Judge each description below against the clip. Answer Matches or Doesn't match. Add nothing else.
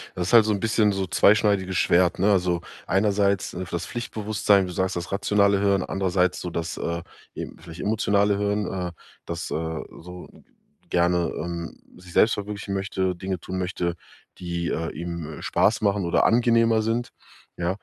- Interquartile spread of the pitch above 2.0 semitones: Matches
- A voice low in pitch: Matches